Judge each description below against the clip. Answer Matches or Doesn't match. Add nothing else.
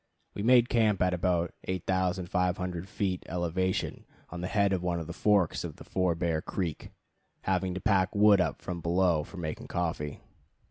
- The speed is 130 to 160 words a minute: Doesn't match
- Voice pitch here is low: Matches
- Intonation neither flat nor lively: Doesn't match